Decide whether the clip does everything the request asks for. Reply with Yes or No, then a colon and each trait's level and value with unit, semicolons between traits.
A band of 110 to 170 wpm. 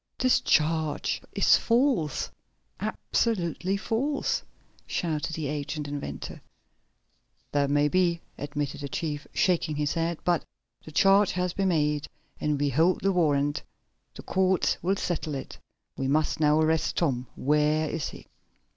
Yes: average, 140 wpm